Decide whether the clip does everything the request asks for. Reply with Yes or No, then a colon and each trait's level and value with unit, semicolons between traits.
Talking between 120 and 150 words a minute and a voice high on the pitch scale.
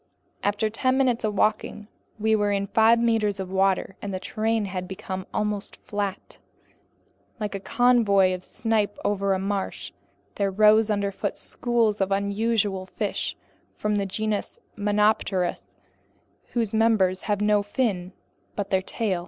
Yes: average, 145 wpm; high, 205 Hz